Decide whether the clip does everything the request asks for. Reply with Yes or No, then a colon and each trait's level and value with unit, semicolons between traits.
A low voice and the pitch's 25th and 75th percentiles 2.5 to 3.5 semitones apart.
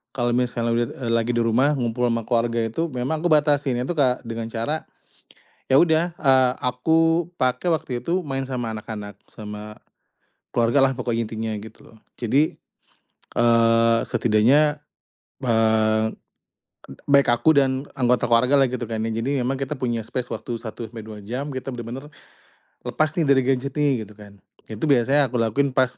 Yes: low, 125 Hz; average, 3.2 semitones